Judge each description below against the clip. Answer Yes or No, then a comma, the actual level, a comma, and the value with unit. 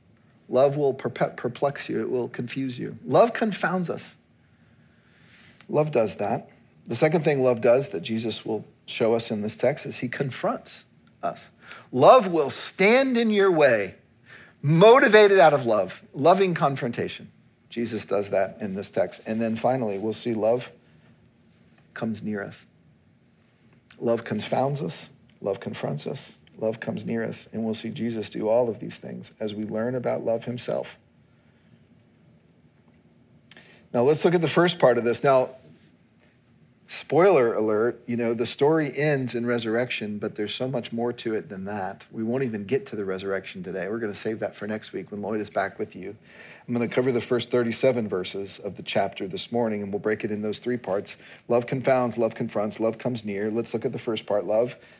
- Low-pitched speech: Yes, low, 120 Hz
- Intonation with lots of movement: No, average, 3.7 semitones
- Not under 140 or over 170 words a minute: No, average, 185 wpm